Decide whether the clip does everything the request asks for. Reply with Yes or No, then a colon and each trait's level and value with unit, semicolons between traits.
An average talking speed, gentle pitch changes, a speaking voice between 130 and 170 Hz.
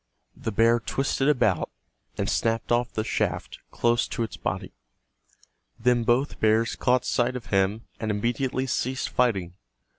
No: average, 145 wpm; narrow, 2.3 semitones; low, 120 Hz